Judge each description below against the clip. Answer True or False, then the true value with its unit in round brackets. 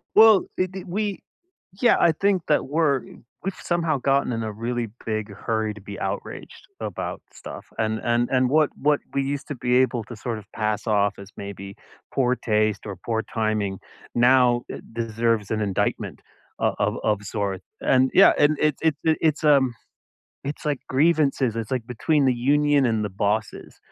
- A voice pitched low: True (125 Hz)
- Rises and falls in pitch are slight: False (5.3 semitones)